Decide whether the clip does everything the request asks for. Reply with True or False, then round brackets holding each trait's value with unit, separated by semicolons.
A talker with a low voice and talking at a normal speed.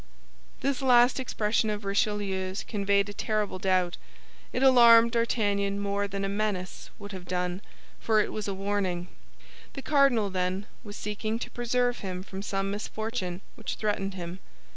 False (205 Hz; 155 wpm)